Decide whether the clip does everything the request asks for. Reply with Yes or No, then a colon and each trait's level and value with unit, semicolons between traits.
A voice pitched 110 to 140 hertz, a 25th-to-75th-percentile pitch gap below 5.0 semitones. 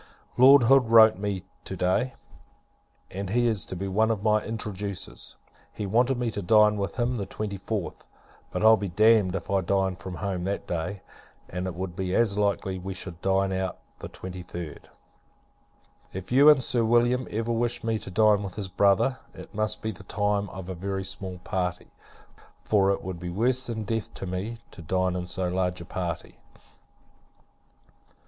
No: low, 100 Hz; average, 3.2 semitones